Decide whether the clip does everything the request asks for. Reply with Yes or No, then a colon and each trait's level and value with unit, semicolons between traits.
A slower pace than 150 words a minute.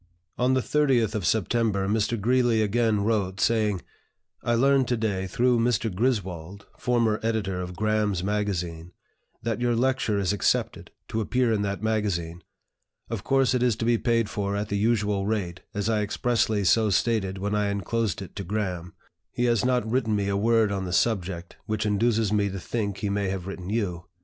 No: average, 185 wpm